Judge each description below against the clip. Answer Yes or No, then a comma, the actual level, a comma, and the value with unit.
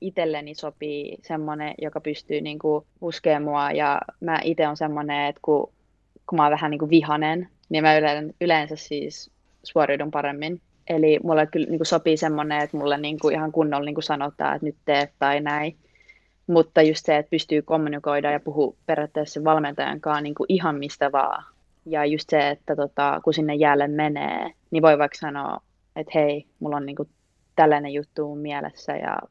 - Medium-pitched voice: Yes, medium, 150 Hz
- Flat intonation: Yes, narrow, 1.2 semitones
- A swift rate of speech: Yes, fast, 170 wpm